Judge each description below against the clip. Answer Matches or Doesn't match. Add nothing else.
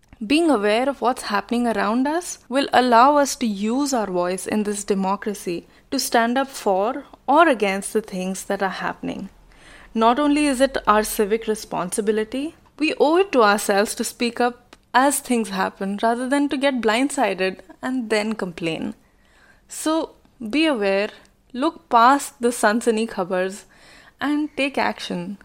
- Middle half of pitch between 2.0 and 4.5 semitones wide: Doesn't match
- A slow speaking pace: Doesn't match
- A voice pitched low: Doesn't match